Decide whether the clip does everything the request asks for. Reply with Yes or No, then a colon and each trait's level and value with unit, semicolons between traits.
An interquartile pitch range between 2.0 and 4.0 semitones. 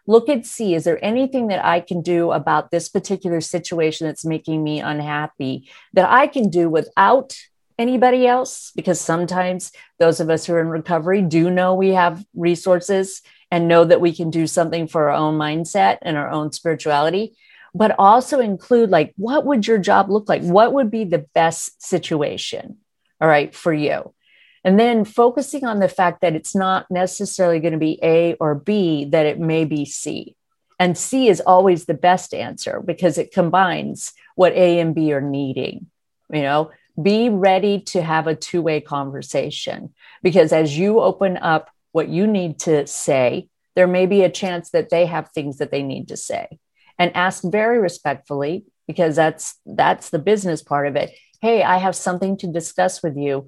Yes: average, 3.5 semitones